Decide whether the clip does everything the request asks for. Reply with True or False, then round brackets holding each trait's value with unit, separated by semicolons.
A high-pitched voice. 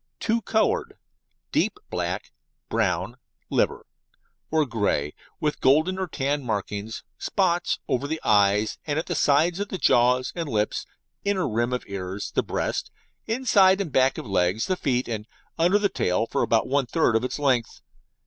False (135 Hz)